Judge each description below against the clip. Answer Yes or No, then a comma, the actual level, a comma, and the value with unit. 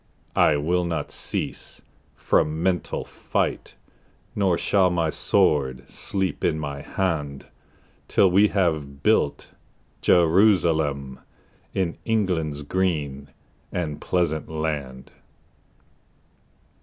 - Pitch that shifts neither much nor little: Yes, average, 4.1 semitones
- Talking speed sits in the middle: No, slow, 95 wpm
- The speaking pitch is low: Yes, very low, 80 Hz